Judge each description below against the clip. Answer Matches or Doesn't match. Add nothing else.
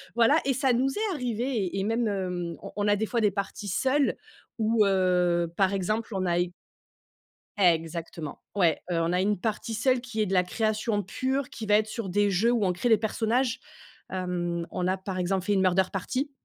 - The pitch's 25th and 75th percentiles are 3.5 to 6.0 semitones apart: Matches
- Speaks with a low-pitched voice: Doesn't match